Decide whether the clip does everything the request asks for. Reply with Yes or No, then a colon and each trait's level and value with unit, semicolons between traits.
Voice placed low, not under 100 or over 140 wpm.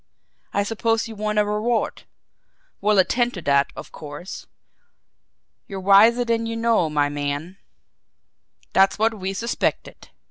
No: high, 210 Hz; slow, 135 wpm